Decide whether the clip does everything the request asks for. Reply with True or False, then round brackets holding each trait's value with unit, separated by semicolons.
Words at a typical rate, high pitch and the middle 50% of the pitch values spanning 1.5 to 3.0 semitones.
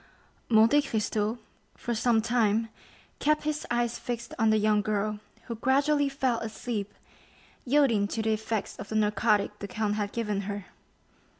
True (155 wpm; 220 Hz; 2.5 semitones)